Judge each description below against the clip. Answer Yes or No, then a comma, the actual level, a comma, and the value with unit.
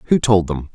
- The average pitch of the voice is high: No, low, 100 Hz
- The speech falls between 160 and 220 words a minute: No, fast, 245 wpm